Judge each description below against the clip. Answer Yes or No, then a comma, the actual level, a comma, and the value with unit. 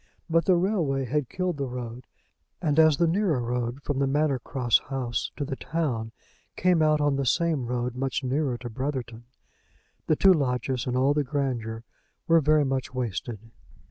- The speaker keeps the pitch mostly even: No, average, 3.8 semitones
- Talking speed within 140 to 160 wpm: No, average, 175 wpm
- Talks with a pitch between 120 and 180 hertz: Yes, low, 135 Hz